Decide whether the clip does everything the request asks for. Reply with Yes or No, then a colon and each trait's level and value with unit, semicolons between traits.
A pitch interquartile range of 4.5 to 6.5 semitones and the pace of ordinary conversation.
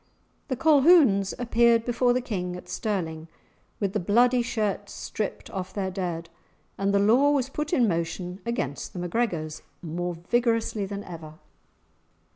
Yes: average, 5.2 semitones; average, 145 wpm